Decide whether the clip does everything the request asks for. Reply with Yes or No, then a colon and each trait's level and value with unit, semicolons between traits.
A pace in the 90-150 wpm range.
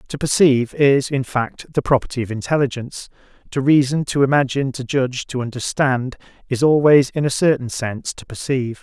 No: average, 170 wpm